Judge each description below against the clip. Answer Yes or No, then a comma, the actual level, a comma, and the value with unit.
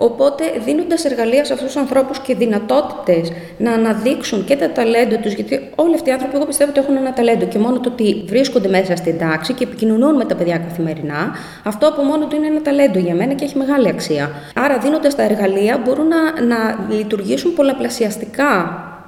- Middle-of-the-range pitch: No, high, 245 Hz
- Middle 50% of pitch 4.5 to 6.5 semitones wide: Yes, average, 5.2 semitones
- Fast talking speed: Yes, fast, 195 wpm